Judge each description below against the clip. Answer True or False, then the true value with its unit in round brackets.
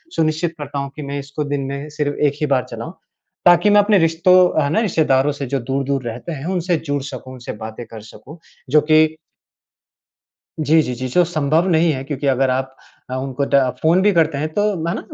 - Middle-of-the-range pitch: True (145 Hz)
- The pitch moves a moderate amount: True (3.3 semitones)